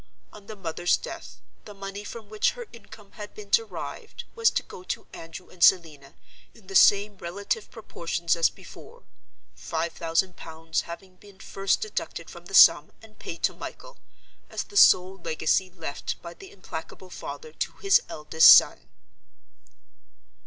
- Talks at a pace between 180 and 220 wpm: No, average, 155 wpm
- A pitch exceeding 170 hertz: Yes, high, 190 Hz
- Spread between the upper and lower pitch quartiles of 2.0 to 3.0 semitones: No, average, 4.0 semitones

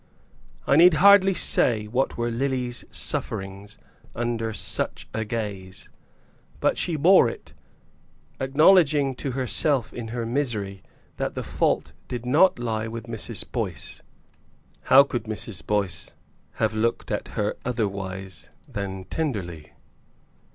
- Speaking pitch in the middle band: No, low, 115 Hz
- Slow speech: Yes, slow, 125 wpm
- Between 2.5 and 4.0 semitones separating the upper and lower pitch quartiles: No, average, 4.7 semitones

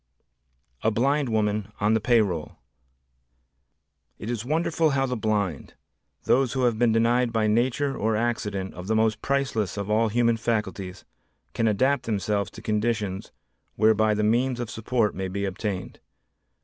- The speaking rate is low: No, average, 155 wpm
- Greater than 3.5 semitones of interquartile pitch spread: No, narrow, 2.6 semitones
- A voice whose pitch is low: Yes, low, 110 Hz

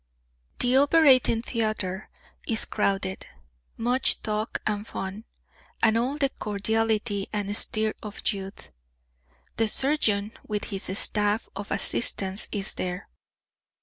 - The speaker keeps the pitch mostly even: Yes, narrow, 2.3 semitones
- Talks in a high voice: Yes, high, 215 Hz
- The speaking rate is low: Yes, slow, 115 wpm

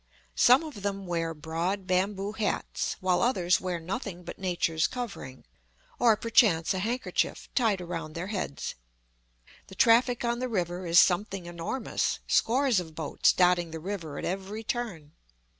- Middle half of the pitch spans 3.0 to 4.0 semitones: No, average, 4.5 semitones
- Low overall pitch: No, medium, 185 Hz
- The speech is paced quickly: No, average, 150 wpm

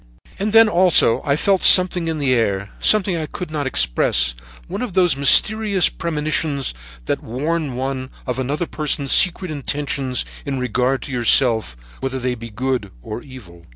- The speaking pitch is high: No, medium, 140 Hz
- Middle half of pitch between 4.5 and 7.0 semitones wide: Yes, average, 5.1 semitones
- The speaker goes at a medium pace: Yes, average, 160 wpm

